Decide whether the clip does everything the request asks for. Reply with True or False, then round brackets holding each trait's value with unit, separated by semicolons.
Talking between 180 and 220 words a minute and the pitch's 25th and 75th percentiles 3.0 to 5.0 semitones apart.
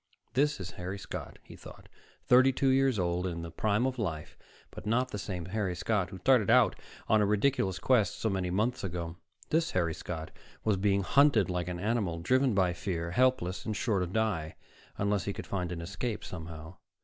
True (200 wpm; 4.4 semitones)